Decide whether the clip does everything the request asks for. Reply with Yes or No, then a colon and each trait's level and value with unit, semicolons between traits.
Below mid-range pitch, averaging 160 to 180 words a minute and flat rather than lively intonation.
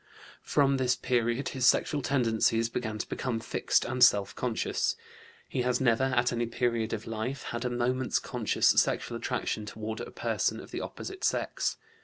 Yes: low, 120 Hz; average, 170 wpm; narrow, 2.2 semitones